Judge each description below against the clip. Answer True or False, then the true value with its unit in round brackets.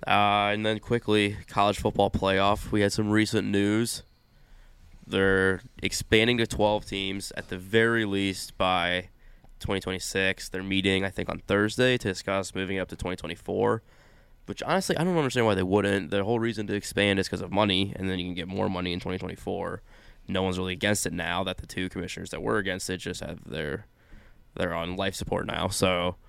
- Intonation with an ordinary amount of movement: False (2.2 semitones)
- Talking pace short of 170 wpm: False (190 wpm)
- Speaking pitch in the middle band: False (95 Hz)